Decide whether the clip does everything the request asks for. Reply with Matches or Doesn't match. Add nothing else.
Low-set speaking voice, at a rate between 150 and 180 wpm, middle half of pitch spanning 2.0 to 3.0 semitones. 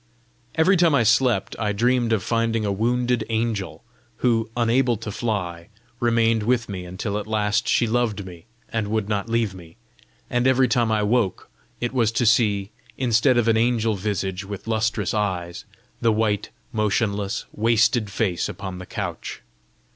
Matches